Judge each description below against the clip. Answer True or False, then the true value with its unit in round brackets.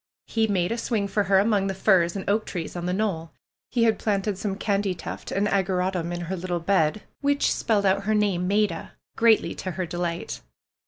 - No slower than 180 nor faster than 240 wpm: True (200 wpm)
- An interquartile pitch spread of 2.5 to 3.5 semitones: True (2.9 semitones)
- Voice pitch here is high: True (195 Hz)